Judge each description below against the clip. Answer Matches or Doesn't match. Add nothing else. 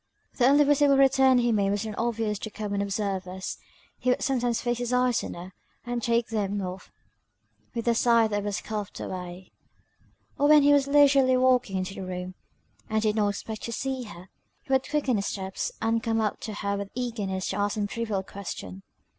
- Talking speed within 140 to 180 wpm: Doesn't match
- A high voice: Matches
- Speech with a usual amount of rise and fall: Matches